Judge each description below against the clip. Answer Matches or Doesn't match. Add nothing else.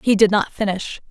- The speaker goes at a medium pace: Doesn't match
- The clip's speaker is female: Matches